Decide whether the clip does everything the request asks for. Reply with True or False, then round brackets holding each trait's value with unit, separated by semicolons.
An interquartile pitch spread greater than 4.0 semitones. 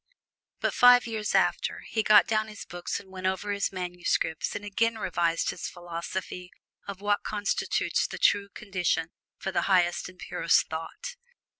False (2.8 semitones)